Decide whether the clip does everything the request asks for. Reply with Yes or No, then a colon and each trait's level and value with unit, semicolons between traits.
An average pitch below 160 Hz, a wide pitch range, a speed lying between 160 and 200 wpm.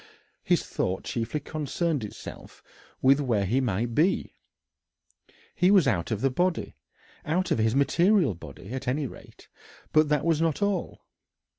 No: medium, 140 Hz; wide, 6.3 semitones; average, 150 wpm